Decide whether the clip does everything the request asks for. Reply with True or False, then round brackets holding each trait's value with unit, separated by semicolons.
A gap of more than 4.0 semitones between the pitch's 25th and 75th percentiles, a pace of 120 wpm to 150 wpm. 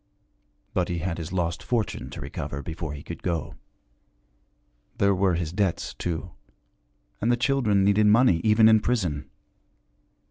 True (4.4 semitones; 145 wpm)